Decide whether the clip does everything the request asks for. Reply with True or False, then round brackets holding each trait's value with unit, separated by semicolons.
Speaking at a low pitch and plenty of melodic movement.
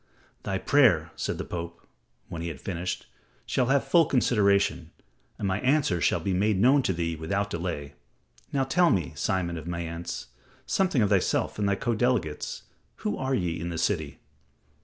True (95 Hz; 6.3 semitones)